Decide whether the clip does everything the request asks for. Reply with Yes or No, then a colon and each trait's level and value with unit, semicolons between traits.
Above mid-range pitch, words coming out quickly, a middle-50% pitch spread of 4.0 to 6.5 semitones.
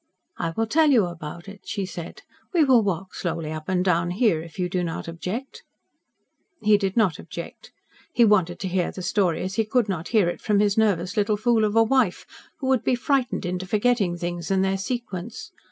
Yes: high, 195 Hz; fast, 210 wpm; average, 4.3 semitones